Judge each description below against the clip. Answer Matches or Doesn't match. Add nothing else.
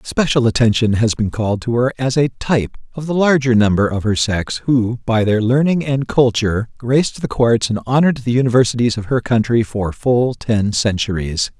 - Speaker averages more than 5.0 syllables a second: Matches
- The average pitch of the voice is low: Matches